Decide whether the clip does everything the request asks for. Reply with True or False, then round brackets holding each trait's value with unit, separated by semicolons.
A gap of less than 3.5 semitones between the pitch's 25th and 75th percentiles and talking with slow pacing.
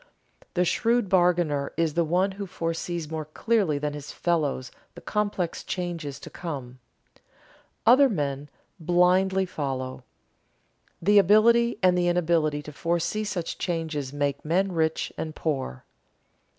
False (4.2 semitones; 130 wpm)